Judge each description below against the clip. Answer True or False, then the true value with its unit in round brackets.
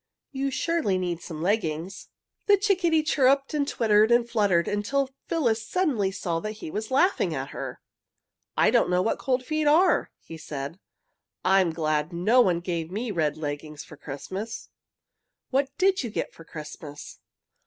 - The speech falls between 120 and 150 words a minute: False (160 wpm)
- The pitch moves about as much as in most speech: False (8.6 semitones)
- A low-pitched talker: False (205 Hz)